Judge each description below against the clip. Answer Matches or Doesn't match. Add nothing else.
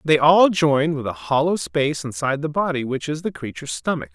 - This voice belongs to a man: Matches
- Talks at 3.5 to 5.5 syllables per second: Doesn't match